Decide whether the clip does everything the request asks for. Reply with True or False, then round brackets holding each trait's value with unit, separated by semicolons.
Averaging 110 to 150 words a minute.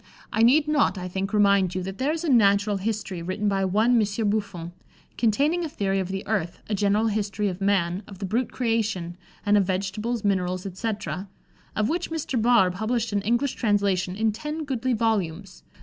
False (190 wpm)